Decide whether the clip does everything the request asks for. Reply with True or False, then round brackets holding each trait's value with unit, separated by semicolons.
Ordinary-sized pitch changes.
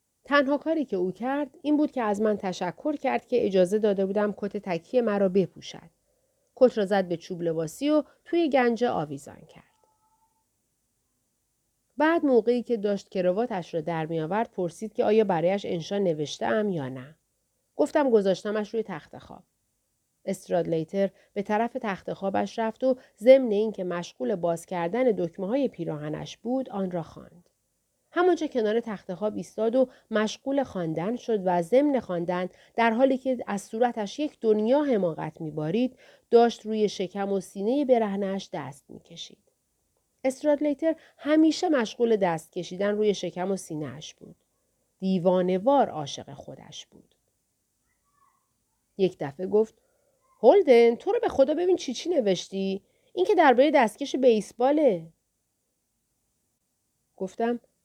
False (6.2 semitones)